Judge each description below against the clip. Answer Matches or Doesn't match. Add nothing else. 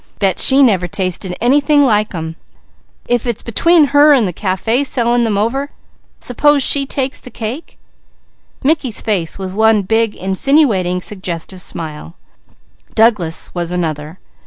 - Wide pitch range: Matches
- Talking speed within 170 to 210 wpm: Doesn't match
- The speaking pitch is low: Doesn't match